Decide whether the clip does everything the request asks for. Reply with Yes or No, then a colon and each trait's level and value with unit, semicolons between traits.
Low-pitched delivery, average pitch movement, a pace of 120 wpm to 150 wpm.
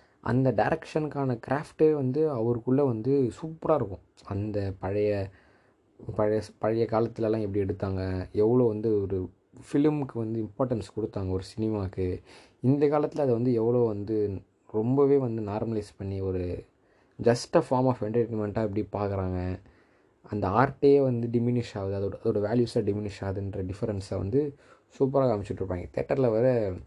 Yes: low, 110 Hz; average, 4.5 semitones; average, 125 wpm